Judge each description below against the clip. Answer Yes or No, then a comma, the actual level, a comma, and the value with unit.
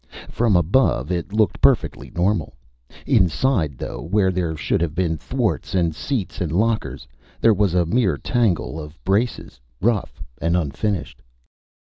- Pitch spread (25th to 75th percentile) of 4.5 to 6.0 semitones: Yes, average, 4.8 semitones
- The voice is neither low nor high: No, very low, 90 Hz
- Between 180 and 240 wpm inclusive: No, average, 140 wpm